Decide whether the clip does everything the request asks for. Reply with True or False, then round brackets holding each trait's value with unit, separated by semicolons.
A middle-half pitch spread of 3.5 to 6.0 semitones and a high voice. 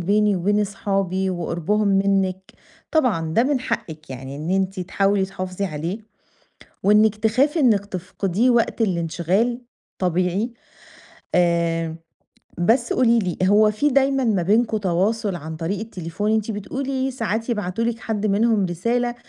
True (4.0 semitones; 200 Hz)